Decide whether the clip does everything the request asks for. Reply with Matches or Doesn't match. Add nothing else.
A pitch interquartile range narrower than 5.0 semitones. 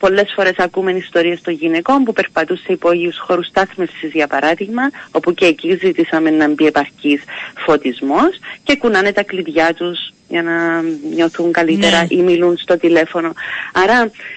Matches